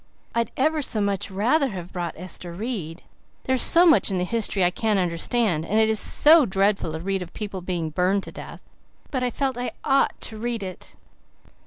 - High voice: Yes, high, 200 Hz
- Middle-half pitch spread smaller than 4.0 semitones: No, average, 5.1 semitones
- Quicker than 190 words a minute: Yes, average, 200 wpm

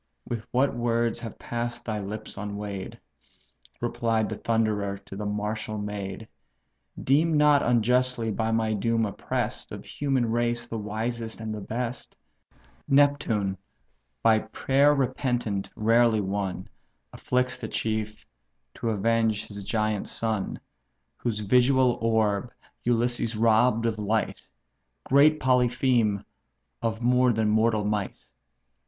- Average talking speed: No, slow, 120 wpm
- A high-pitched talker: No, low, 115 Hz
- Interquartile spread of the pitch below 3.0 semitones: Yes, narrow, 2.5 semitones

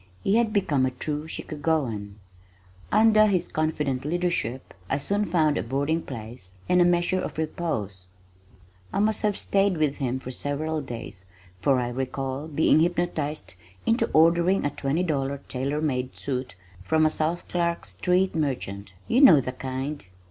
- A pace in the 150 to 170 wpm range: Yes, average, 155 wpm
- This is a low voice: No, medium, 150 Hz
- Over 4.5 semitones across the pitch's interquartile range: Yes, average, 4.9 semitones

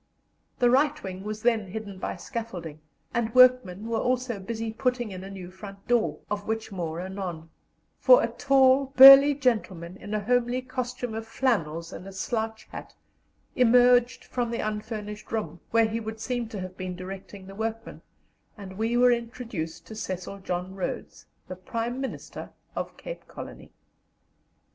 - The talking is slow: No, average, 160 wpm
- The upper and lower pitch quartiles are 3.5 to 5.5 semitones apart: Yes, average, 4.4 semitones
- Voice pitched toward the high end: Yes, high, 220 Hz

